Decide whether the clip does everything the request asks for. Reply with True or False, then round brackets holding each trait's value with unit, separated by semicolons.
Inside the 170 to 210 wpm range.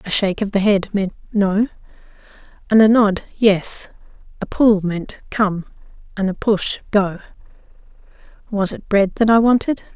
False (150 wpm)